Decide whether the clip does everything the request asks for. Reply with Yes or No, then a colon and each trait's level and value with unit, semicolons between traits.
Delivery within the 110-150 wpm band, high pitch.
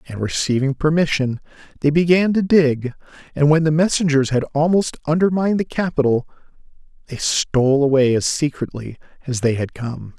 No: average, 145 wpm; medium, 145 Hz